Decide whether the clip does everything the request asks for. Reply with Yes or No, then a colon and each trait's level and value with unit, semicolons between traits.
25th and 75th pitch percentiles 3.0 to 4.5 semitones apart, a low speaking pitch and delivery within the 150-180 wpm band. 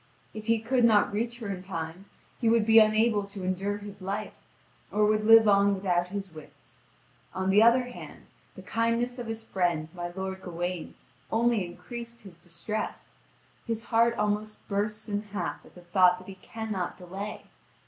No: average, 3.4 semitones; high, 205 Hz; average, 175 wpm